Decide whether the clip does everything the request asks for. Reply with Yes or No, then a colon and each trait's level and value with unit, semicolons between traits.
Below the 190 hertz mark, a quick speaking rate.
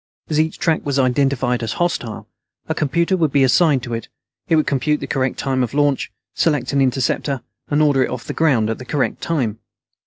Yes: low, 135 Hz; fast, 210 wpm